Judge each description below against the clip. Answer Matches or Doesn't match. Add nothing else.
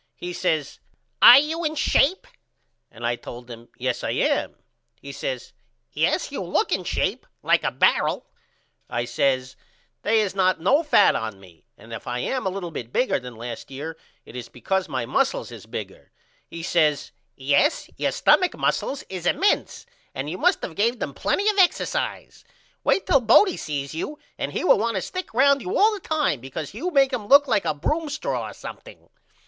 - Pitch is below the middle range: Doesn't match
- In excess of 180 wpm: Matches